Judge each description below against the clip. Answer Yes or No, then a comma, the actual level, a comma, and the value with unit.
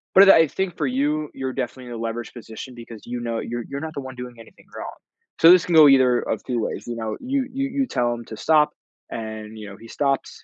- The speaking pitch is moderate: No, low, 130 Hz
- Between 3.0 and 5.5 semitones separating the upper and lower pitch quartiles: Yes, average, 4.7 semitones